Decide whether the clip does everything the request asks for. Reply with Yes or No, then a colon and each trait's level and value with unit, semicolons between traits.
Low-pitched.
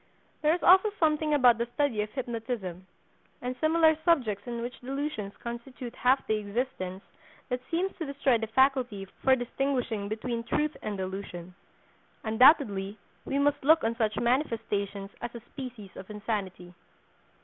No: high, 240 Hz